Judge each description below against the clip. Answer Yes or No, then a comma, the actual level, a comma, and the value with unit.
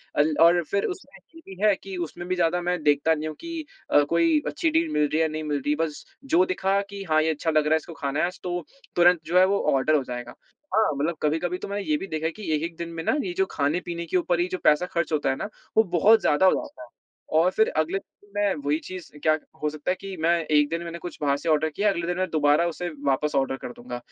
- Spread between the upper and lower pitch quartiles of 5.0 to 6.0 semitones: No, average, 3.5 semitones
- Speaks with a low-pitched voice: No, medium, 170 Hz